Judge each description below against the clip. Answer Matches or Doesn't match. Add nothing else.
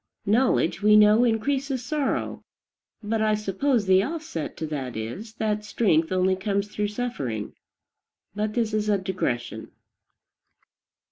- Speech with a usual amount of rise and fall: Matches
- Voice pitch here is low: Doesn't match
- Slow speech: Matches